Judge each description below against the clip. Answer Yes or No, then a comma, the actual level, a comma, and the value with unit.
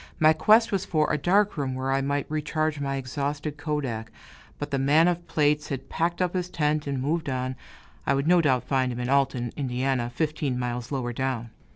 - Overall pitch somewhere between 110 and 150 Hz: Yes, medium, 140 Hz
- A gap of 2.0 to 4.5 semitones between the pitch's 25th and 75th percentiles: Yes, average, 3.2 semitones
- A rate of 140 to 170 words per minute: No, fast, 205 wpm